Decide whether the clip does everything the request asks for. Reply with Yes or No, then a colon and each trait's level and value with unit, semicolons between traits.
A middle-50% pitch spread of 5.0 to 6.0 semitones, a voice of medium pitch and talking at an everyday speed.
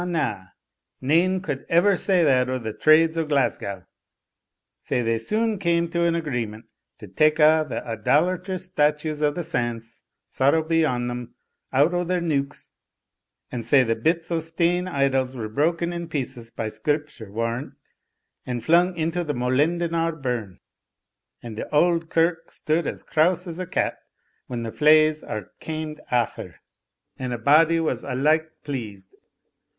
Yes: average, 5.3 semitones; medium, 150 Hz; average, 155 wpm